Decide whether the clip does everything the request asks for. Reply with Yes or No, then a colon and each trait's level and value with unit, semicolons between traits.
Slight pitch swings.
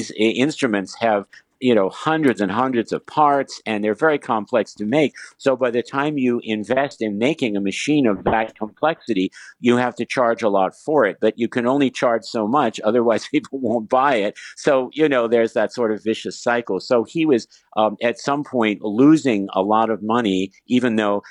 No: average, 3.8 semitones